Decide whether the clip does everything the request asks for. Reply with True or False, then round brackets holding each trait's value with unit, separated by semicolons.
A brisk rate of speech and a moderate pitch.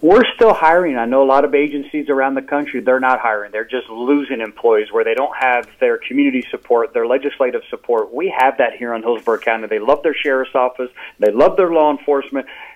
True (215 wpm; 145 Hz)